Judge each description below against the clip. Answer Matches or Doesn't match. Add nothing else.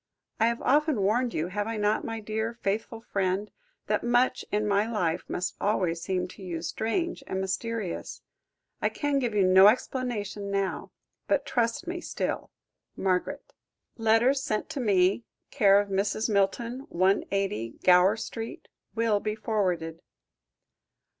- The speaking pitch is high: Matches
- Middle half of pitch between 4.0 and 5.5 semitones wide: Doesn't match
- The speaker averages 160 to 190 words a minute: Doesn't match